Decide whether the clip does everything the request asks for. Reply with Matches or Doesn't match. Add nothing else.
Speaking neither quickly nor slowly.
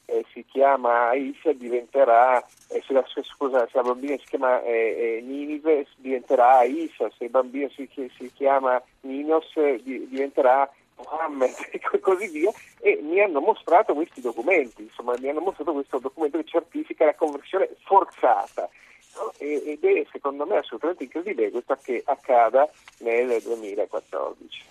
Matches